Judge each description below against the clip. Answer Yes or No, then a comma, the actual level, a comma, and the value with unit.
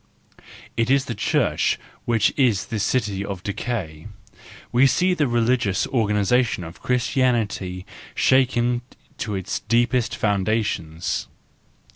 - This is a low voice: Yes, low, 115 Hz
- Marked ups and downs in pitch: No, average, 3.9 semitones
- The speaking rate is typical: No, slow, 110 wpm